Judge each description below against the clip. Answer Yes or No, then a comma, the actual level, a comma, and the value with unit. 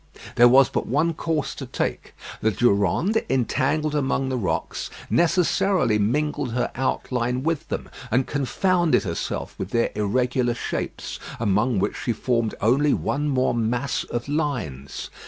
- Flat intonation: No, average, 4.2 semitones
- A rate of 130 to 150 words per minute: Yes, average, 140 wpm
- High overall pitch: No, low, 130 Hz